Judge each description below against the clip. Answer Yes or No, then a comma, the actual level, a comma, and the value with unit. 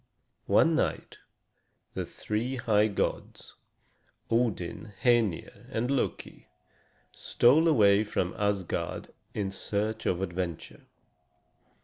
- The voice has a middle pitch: No, low, 105 Hz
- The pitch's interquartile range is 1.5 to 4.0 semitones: Yes, average, 3.5 semitones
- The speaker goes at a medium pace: No, slow, 90 wpm